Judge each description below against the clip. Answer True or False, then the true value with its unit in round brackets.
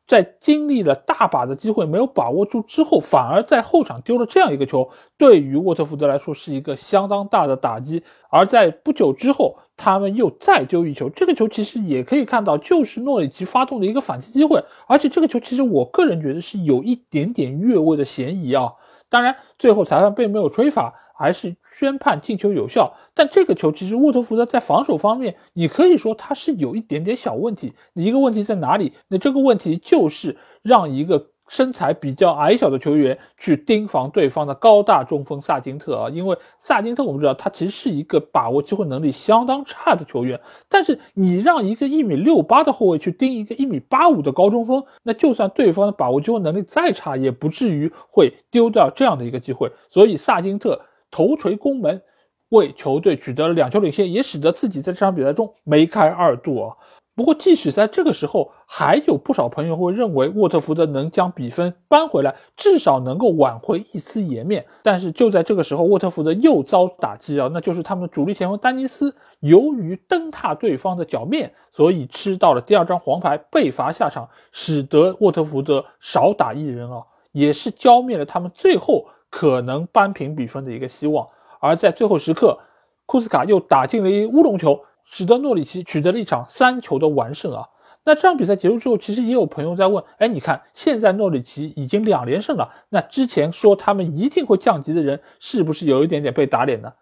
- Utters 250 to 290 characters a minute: False (320 characters per minute)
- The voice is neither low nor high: False (200 Hz)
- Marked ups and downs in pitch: True (8.4 semitones)